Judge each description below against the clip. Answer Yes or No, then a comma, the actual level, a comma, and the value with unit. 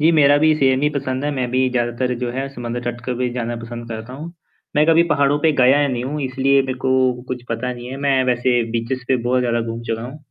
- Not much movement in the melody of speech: Yes, narrow, 2.3 semitones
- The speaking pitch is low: Yes, low, 130 Hz